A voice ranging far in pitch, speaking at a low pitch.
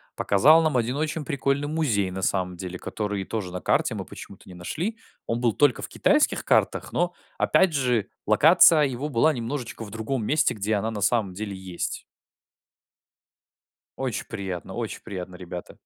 Yes: wide, 7.0 semitones; low, 115 Hz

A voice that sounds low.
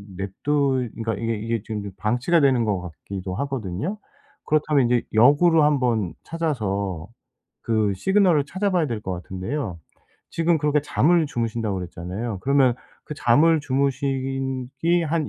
Yes: low, 130 Hz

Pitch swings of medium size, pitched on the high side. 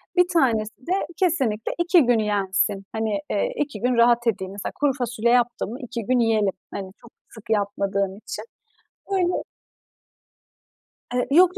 Yes: average, 4.2 semitones; high, 235 Hz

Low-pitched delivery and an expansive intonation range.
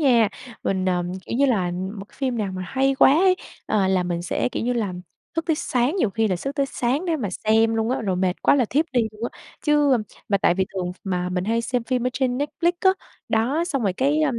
No: high, 235 Hz; wide, 6.3 semitones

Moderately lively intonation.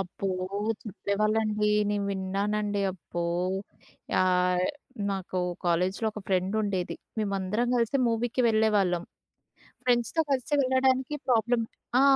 Yes: average, 3.5 semitones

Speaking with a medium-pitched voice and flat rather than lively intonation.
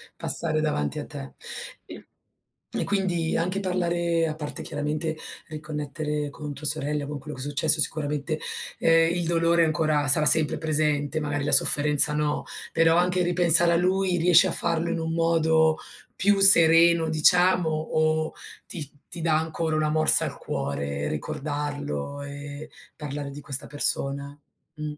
Yes: medium, 155 Hz; narrow, 2.3 semitones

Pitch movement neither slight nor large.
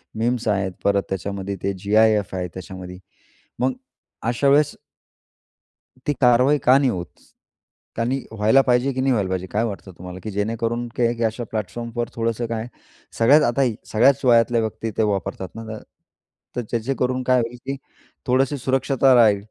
Yes: average, 3.7 semitones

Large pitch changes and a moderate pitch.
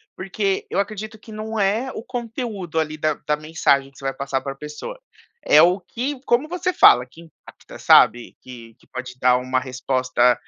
Yes: wide, 8.8 semitones; medium, 160 Hz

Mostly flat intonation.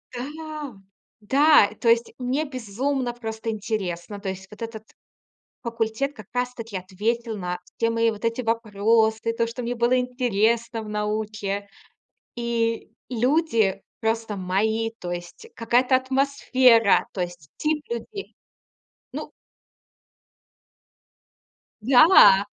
No: average, 3.0 semitones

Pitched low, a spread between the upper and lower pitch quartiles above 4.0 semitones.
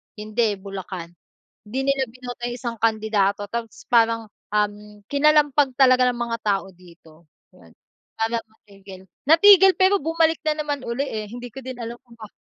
No: high, 230 Hz; average, 4.5 semitones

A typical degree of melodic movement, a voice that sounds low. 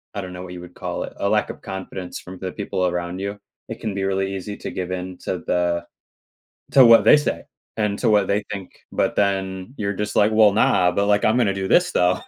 No: narrow, 2.1 semitones; very low, 95 Hz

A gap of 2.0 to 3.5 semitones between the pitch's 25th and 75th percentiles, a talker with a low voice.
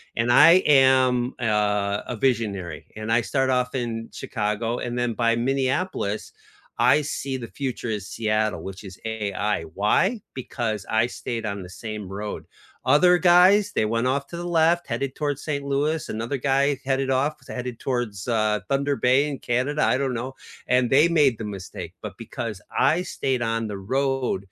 No: average, 4.3 semitones; low, 125 Hz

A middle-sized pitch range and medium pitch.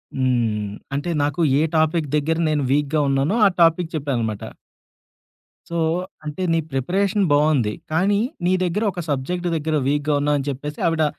Yes: average, 3.5 semitones; medium, 150 Hz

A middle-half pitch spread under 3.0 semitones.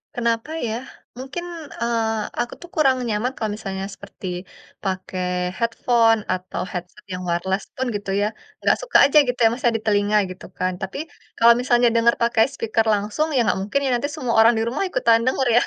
No: average, 3.3 semitones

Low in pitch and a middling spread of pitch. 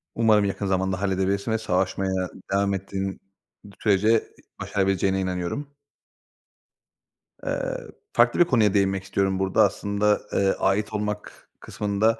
No: low, 100 Hz; narrow, 1.6 semitones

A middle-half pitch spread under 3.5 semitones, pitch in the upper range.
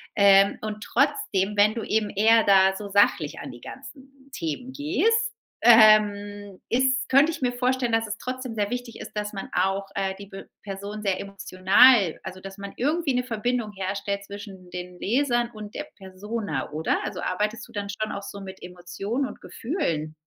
No: average, 3.8 semitones; high, 205 Hz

